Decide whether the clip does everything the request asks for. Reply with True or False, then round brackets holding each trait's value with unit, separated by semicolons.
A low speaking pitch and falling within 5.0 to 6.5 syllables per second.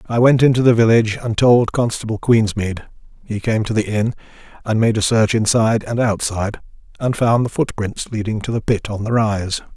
True (110 Hz; 5.5 syllables/s)